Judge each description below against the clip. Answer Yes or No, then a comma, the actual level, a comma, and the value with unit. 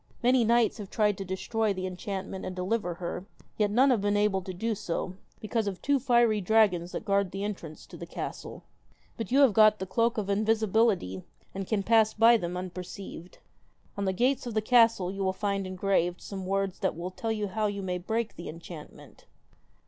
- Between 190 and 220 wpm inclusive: Yes, average, 200 wpm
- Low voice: No, high, 200 Hz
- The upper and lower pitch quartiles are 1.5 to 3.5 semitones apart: Yes, average, 3.1 semitones